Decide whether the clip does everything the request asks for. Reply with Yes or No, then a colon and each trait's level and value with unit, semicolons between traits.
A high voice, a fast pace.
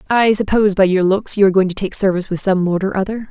Yes: high, 195 Hz; fast, 290 wpm